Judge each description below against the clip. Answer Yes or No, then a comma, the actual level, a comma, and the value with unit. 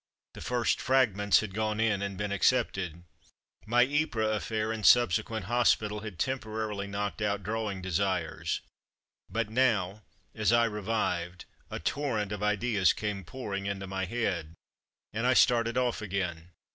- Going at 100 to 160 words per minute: Yes, average, 150 wpm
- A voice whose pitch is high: No, low, 105 Hz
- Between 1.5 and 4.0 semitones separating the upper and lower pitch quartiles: Yes, average, 2.8 semitones